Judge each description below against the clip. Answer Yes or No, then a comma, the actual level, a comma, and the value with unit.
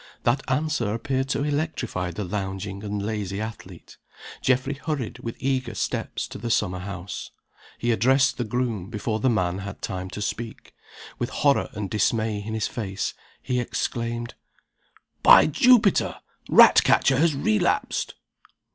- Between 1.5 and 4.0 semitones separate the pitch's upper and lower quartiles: No, average, 4.5 semitones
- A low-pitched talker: Yes, low, 115 Hz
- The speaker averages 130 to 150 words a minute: Yes, average, 140 wpm